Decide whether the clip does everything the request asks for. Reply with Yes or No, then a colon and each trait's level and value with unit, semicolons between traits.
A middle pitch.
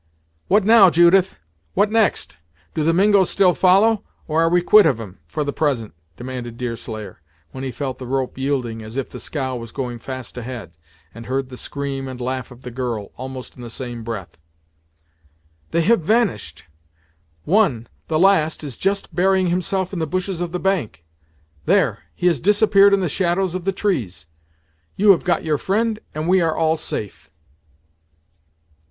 Yes: medium, 155 Hz